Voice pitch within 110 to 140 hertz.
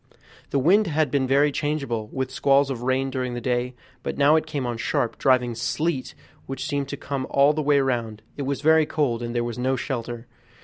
Yes: low, 135 Hz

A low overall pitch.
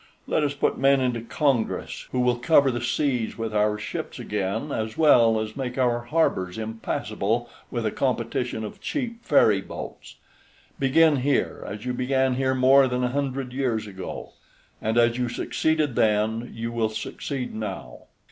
Yes: low, 125 Hz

